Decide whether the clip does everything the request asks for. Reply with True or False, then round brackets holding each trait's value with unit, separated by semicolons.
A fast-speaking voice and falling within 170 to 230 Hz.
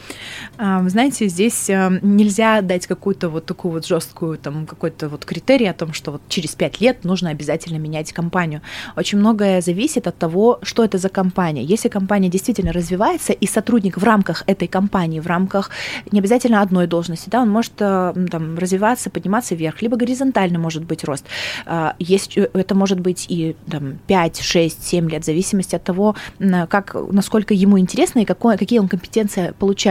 True (170 wpm; 190 Hz)